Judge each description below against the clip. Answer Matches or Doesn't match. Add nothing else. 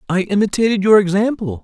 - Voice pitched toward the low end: Doesn't match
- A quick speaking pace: Doesn't match